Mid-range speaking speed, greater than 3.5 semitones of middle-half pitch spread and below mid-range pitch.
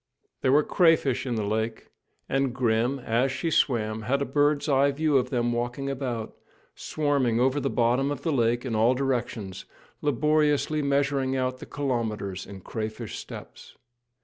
No: average, 165 wpm; average, 3.2 semitones; low, 130 Hz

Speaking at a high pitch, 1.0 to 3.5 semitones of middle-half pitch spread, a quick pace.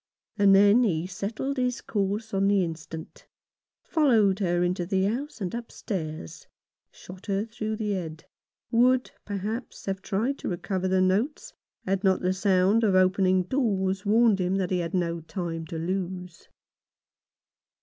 No: high, 195 Hz; average, 3.0 semitones; average, 150 wpm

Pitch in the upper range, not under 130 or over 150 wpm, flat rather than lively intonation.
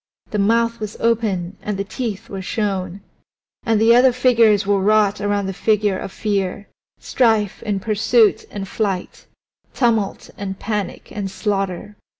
Yes: high, 205 Hz; average, 145 wpm; narrow, 2.2 semitones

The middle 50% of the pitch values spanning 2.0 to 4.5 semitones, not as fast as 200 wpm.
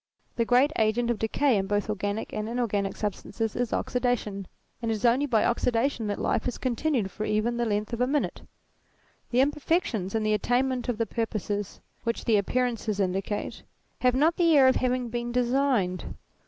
Yes: average, 3.0 semitones; average, 180 wpm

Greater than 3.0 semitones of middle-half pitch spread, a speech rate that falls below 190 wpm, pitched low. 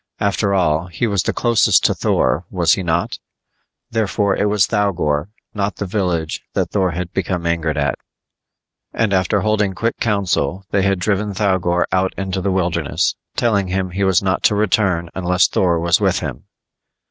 No: average, 2.7 semitones; average, 170 wpm; very low, 95 Hz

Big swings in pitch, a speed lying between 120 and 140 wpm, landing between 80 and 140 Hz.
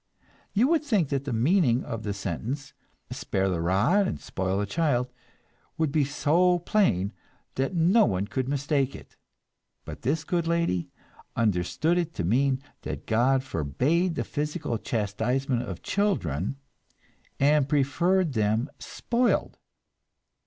Yes: wide, 7.3 semitones; slow, 135 wpm; low, 135 Hz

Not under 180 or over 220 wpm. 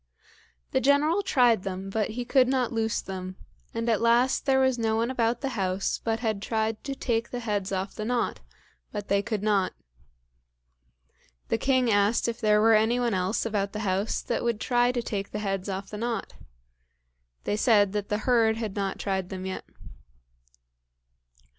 Yes: average, 185 wpm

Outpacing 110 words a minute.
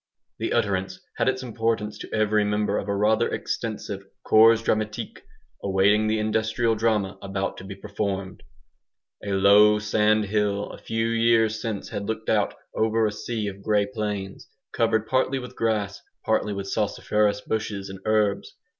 Yes: average, 155 wpm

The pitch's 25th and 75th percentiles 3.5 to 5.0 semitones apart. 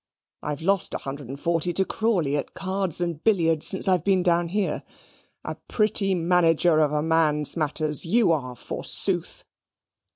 Yes: average, 3.9 semitones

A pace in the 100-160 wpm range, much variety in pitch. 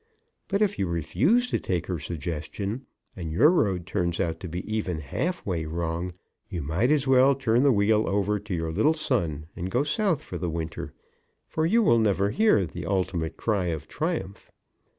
No: average, 185 wpm; wide, 7.7 semitones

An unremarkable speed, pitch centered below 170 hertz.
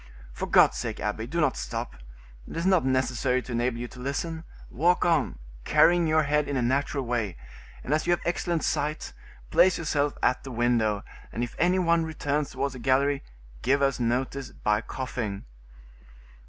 Yes: average, 175 wpm; low, 135 Hz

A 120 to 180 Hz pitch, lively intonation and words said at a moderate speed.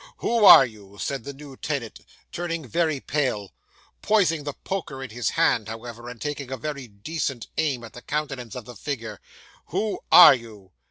No: low, 135 Hz; average, 4.7 semitones; average, 175 wpm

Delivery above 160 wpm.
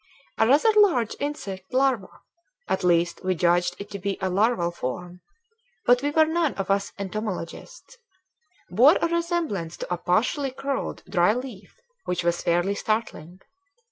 No: average, 150 wpm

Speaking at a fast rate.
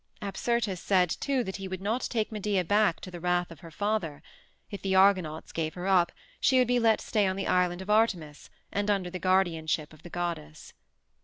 Yes: fast, 210 wpm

